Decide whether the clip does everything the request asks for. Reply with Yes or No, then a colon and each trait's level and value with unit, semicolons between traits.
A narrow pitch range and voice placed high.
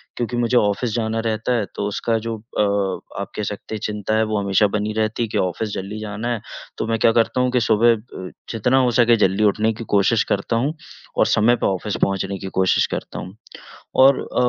No: narrow, 2.3 semitones; low, 110 Hz